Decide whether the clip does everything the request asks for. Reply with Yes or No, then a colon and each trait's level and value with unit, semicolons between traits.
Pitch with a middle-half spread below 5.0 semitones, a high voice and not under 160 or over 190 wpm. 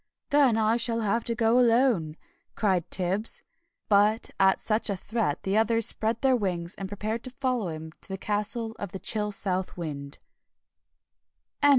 Yes: average, 3.4 semitones; high, 210 Hz; average, 165 wpm